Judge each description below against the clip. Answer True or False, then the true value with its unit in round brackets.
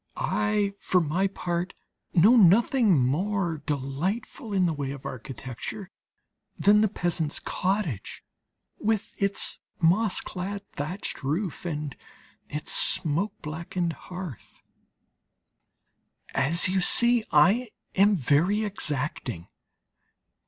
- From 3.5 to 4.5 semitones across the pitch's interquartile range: False (5.3 semitones)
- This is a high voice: False (180 Hz)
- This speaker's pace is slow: True (105 wpm)